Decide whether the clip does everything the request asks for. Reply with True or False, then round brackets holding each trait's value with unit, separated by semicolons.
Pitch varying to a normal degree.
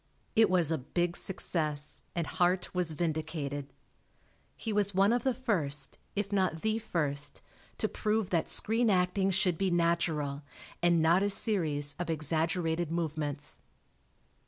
True (3.9 semitones)